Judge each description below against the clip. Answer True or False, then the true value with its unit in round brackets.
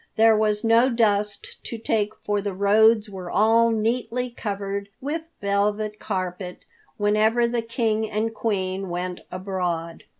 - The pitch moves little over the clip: True (2.3 semitones)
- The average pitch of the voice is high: True (210 Hz)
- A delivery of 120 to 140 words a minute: True (135 wpm)